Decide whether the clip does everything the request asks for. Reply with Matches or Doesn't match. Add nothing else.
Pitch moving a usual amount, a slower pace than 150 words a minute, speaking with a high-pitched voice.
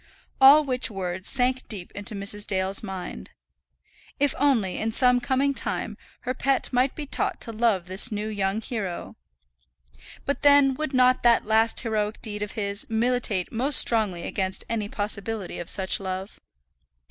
Doesn't match